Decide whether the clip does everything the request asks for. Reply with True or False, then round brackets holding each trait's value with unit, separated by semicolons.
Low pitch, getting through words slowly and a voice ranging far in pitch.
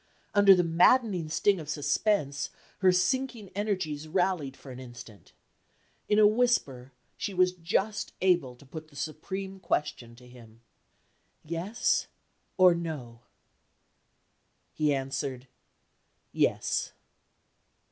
False (165 Hz; 110 wpm; 6.0 semitones)